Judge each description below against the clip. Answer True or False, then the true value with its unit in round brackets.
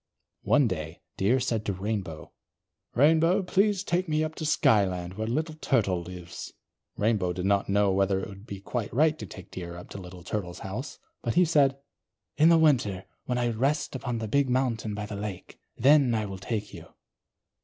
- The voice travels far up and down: True (6.6 semitones)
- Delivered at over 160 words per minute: True (190 wpm)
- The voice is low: True (110 Hz)